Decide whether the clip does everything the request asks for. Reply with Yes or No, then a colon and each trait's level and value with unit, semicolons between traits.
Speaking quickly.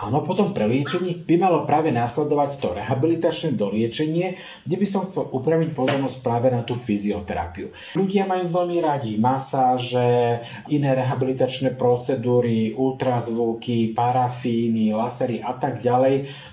No: average, 125 wpm